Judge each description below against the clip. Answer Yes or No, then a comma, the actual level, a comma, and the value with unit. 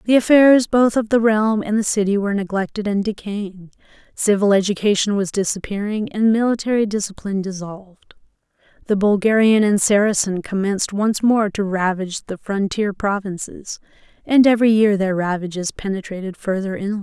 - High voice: Yes, high, 205 Hz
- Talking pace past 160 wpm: No, average, 145 wpm